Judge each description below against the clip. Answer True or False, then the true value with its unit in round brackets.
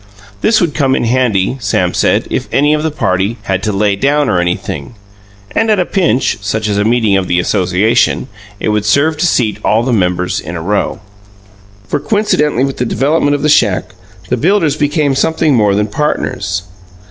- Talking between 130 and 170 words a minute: False (195 wpm)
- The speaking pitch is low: True (120 Hz)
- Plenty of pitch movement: True (6.7 semitones)